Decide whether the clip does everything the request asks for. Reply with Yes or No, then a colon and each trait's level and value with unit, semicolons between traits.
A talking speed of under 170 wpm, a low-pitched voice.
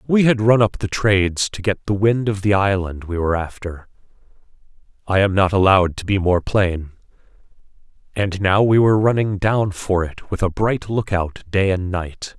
No: average, 180 wpm; low, 100 Hz